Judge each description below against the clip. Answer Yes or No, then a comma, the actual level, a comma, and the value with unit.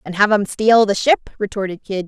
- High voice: Yes, high, 205 Hz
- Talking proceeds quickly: Yes, fast, 230 wpm